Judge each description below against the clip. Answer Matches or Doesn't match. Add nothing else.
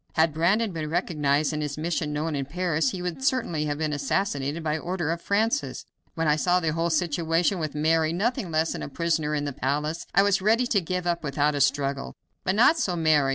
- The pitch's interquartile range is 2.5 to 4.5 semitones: Matches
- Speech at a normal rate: Doesn't match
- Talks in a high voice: Doesn't match